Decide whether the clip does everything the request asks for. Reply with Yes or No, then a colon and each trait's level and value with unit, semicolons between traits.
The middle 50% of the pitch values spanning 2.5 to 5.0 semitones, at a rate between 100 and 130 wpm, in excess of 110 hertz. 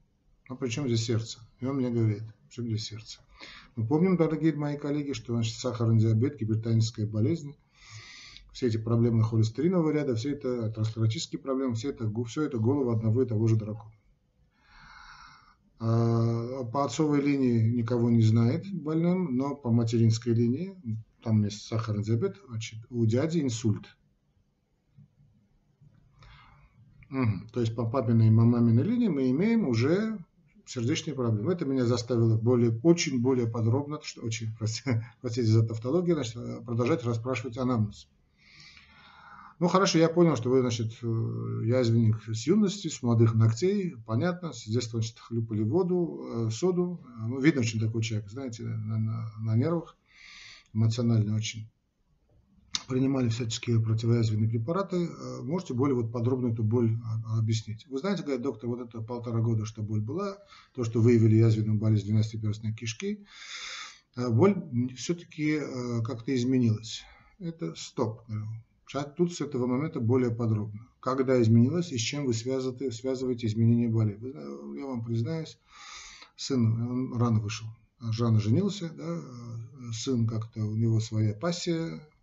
No: average, 3.7 semitones; average, 140 wpm; low, 120 Hz